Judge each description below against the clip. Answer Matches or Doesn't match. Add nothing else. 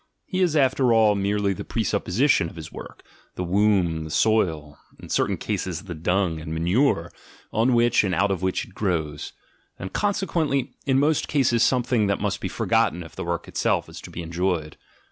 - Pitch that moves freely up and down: Matches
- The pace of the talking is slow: Doesn't match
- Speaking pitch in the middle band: Doesn't match